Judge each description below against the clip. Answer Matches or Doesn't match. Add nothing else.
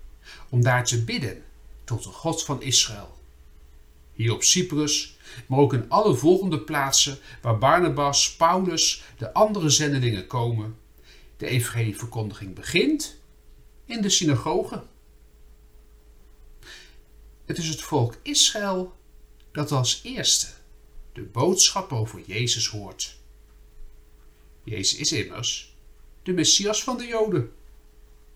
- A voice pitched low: Matches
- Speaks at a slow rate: Matches